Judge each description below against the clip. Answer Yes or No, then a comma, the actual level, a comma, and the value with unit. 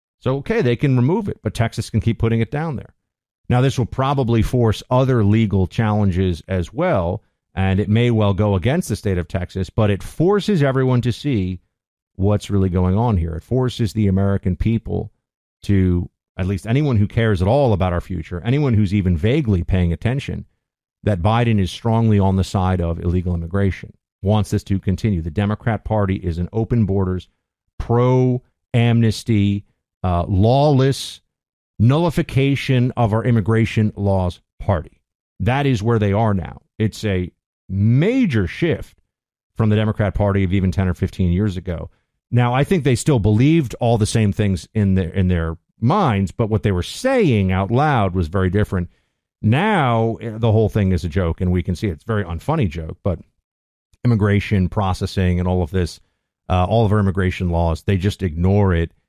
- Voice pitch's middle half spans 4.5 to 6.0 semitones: No, average, 3.9 semitones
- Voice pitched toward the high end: No, low, 105 Hz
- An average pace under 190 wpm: Yes, average, 180 wpm